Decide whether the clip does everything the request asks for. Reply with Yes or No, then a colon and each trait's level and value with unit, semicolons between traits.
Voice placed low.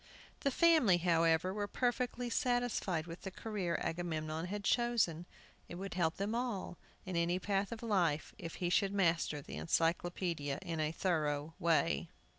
No: medium, 175 Hz